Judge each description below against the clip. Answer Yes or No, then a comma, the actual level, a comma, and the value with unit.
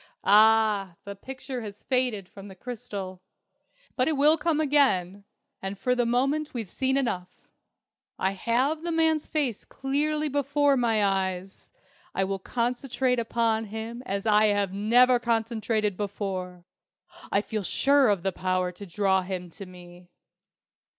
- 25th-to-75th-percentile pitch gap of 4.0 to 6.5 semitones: Yes, average, 5.1 semitones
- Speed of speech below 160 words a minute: Yes, average, 145 wpm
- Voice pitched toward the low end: No, high, 220 Hz